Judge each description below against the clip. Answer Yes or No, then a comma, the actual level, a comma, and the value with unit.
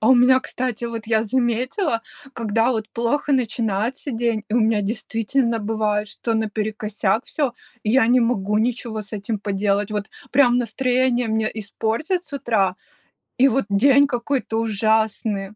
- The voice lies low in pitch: No, high, 225 Hz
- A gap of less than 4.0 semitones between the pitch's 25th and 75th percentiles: Yes, average, 2.7 semitones